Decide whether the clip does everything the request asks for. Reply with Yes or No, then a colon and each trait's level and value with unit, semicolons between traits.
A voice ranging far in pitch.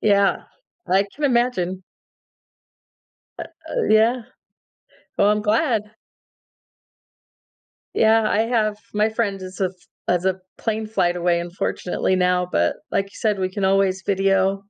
No: average, 2.8 semitones